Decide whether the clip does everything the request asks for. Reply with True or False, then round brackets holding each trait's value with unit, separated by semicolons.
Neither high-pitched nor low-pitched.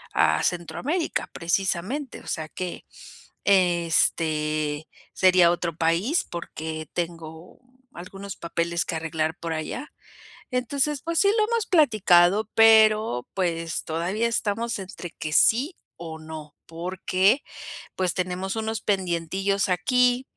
True (180 Hz)